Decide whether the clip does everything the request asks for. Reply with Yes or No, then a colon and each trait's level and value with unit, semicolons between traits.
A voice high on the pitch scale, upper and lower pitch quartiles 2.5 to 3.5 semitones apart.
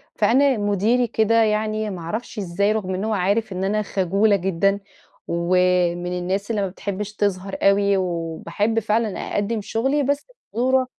Yes: high, 205 Hz; average, 2.9 semitones